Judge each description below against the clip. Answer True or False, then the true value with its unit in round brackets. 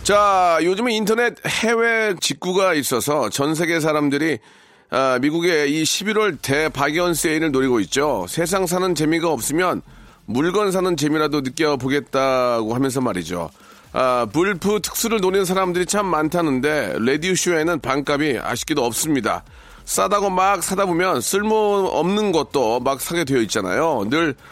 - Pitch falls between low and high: True (170 Hz)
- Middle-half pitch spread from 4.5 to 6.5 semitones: True (5.3 semitones)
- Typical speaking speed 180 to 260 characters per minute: False (315 characters per minute)